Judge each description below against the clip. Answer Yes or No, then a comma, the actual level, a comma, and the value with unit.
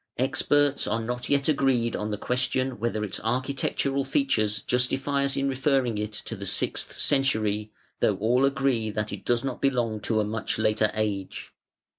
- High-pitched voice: No, low, 125 Hz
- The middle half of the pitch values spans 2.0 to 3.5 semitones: No, average, 4.1 semitones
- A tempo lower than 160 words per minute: No, average, 170 wpm